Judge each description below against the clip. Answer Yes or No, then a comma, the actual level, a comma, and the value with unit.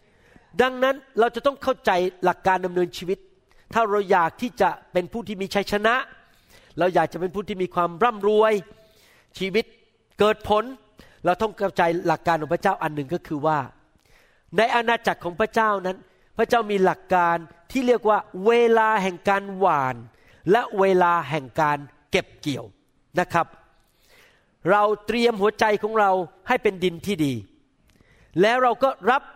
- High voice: Yes, high, 195 Hz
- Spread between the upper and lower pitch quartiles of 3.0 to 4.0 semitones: No, average, 4.4 semitones